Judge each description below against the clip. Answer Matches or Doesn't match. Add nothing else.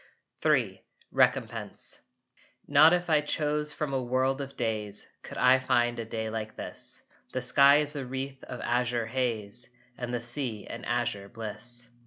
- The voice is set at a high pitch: Doesn't match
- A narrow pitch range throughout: Doesn't match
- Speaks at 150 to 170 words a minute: Matches